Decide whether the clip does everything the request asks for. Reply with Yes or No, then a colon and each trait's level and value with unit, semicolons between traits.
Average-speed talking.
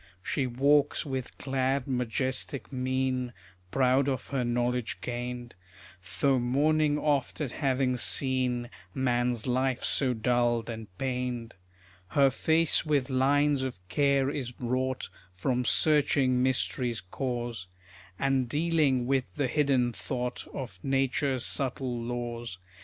No: slow, 120 wpm